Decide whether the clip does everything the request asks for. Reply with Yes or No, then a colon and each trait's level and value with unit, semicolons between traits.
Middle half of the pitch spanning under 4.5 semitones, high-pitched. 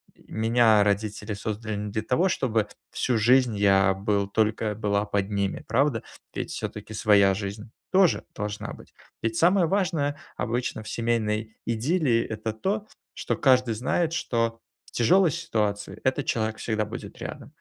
No: average, 3.5 semitones; low, 110 Hz